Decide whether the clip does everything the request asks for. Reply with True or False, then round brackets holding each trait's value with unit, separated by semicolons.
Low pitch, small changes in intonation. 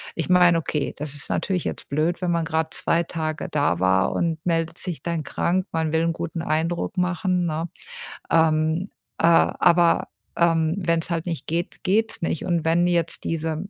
False (165 Hz; 1.6 semitones)